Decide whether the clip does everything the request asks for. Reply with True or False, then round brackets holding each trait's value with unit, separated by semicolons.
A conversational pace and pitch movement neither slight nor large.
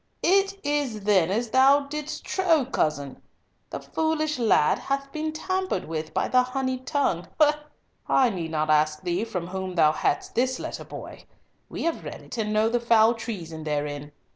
False (170 wpm; 9.0 semitones)